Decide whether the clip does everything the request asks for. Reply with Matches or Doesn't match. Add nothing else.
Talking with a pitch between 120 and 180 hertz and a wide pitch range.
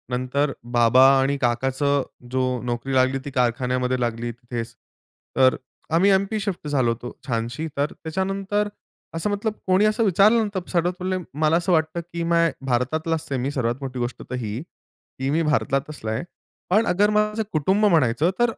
Matches